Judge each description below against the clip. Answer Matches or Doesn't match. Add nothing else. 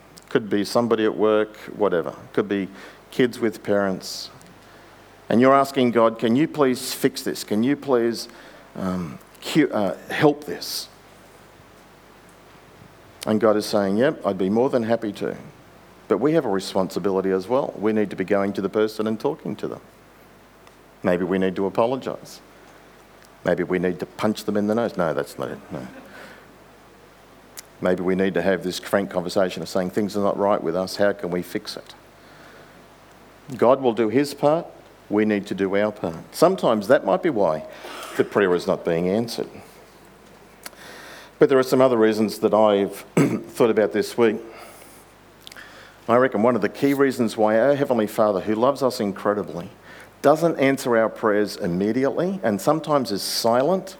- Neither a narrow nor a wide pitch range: Matches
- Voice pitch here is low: Matches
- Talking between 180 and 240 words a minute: Doesn't match